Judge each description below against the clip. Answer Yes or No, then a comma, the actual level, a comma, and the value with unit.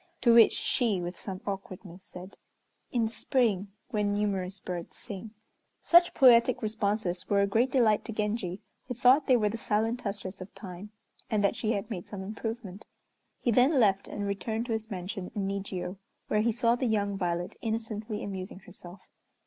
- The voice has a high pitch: Yes, high, 210 Hz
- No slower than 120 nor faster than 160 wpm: No, average, 180 wpm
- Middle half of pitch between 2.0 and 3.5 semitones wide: Yes, average, 3.0 semitones